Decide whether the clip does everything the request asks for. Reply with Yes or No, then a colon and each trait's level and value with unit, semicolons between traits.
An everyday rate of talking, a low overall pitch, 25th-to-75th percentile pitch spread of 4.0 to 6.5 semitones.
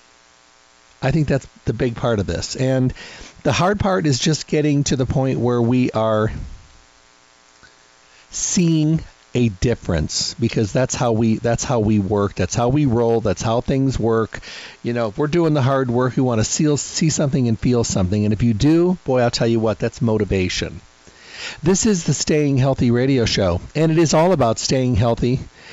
Yes: average, 185 wpm; low, 120 Hz; average, 4.7 semitones